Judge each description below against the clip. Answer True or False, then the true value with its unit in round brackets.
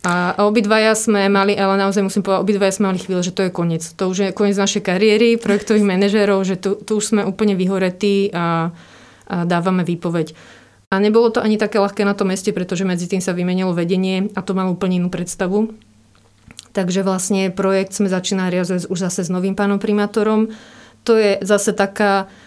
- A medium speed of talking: False (190 wpm)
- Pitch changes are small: True (2.0 semitones)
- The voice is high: True (195 Hz)